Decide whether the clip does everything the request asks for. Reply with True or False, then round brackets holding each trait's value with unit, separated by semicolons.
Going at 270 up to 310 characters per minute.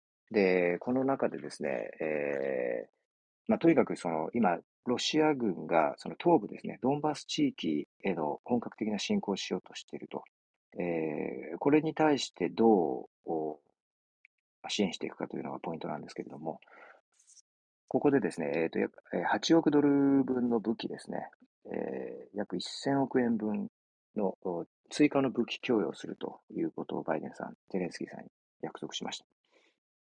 True (305 characters per minute)